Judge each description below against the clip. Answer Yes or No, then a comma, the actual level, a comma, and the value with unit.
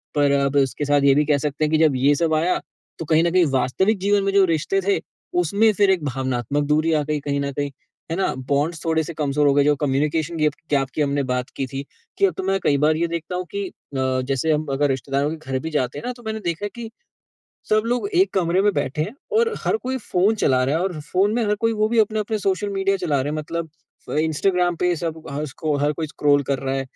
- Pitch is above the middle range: No, medium, 155 Hz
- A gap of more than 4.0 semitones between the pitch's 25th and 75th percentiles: Yes, average, 5.0 semitones